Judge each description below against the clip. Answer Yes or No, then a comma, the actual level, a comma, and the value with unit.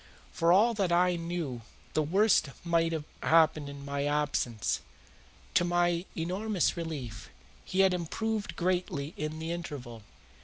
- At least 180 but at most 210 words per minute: No, average, 140 wpm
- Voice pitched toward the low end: No, medium, 165 Hz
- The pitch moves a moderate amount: Yes, average, 3.5 semitones